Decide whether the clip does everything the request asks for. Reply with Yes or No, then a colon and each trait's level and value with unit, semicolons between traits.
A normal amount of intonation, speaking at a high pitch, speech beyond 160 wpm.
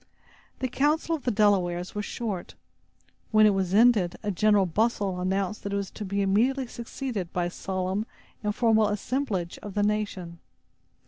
Yes: average, 3.2 semitones; high, 205 Hz; average, 170 wpm